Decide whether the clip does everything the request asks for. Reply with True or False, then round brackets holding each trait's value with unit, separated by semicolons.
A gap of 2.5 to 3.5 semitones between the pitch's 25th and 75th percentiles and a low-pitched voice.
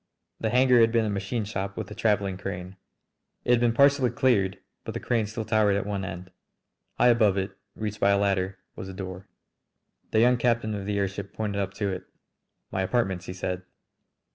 True (3.0 semitones; 100 Hz)